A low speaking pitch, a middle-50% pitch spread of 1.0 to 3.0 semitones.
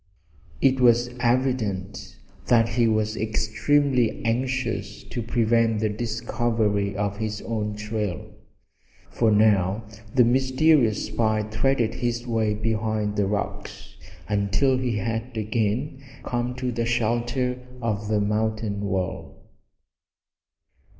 Yes: low, 110 Hz; narrow, 2.4 semitones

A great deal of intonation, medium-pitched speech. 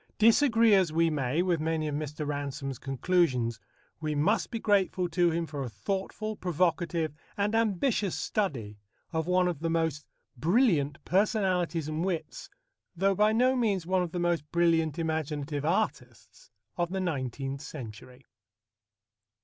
No: average, 4.3 semitones; medium, 165 Hz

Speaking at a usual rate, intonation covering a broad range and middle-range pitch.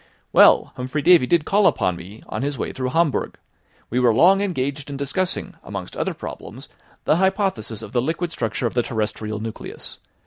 No: average, 180 wpm; wide, 7.2 semitones; low, 130 Hz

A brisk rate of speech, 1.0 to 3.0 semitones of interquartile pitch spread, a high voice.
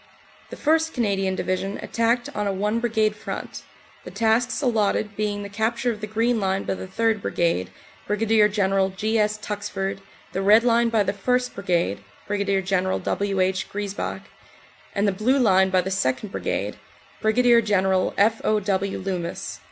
No: average, 165 wpm; narrow, 2.6 semitones; high, 205 Hz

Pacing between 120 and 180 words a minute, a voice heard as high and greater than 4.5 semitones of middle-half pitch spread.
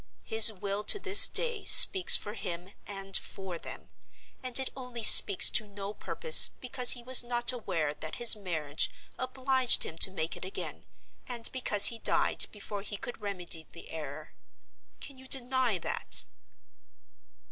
Yes: average, 160 wpm; high, 215 Hz; average, 5.2 semitones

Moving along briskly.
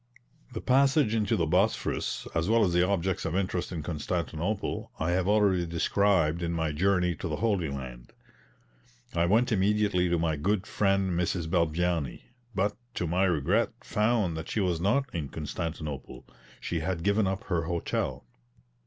No: average, 160 wpm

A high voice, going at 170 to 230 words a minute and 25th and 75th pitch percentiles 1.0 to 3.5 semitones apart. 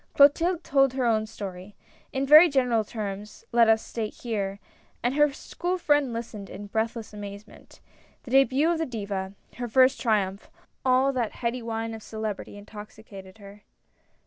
No: high, 225 Hz; average, 175 wpm; average, 4.3 semitones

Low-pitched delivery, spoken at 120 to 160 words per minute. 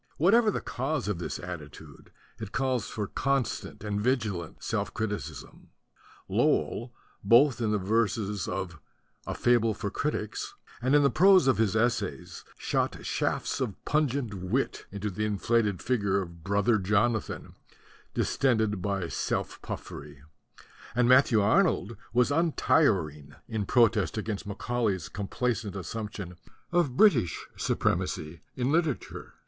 Yes: low, 110 Hz; slow, 135 wpm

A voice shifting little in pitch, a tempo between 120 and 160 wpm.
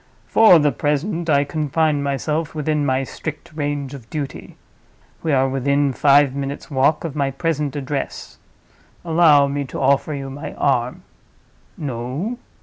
Yes: narrow, 2.2 semitones; average, 145 wpm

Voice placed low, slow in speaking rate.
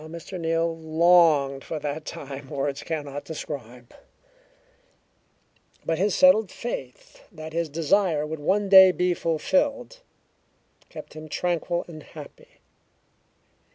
No: medium, 160 Hz; slow, 120 wpm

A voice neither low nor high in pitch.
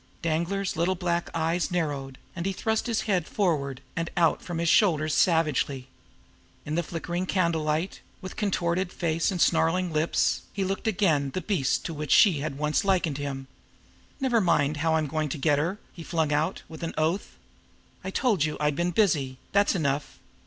Yes: medium, 165 Hz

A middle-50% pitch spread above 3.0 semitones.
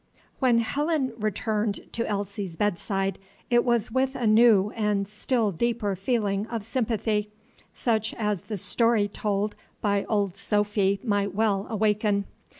No: narrow, 2.4 semitones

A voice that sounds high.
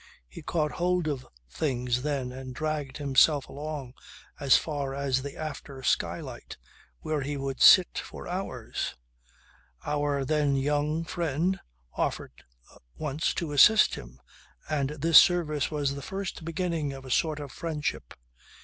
No: medium, 145 Hz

